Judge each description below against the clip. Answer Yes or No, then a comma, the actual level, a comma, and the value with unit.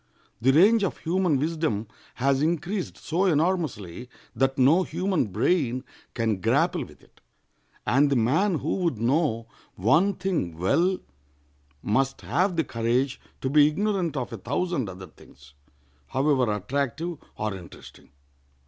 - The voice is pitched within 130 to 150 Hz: Yes, medium, 140 Hz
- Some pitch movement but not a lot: No, wide, 6.9 semitones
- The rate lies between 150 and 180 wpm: No, slow, 135 wpm